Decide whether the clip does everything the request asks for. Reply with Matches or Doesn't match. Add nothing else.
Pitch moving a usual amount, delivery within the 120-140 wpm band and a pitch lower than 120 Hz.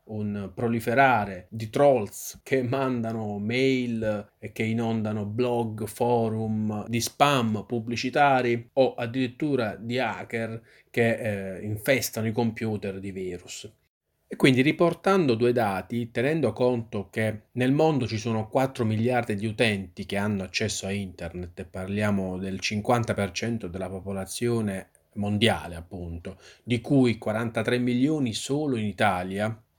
Matches